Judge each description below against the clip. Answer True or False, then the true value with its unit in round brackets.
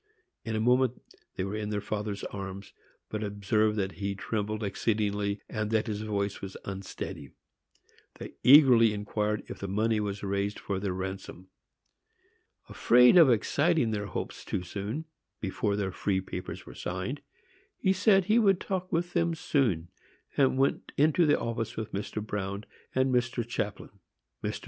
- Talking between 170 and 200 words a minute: False (160 wpm)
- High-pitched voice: False (105 Hz)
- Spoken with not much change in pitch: False (4.0 semitones)